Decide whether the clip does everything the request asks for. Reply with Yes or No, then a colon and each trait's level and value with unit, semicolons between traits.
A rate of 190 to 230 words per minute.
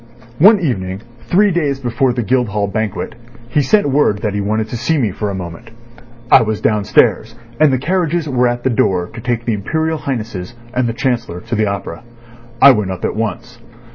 Yes: average, 200 wpm